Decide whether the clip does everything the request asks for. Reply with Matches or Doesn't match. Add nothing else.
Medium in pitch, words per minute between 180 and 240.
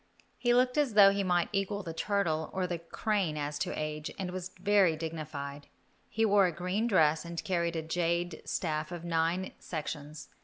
Matches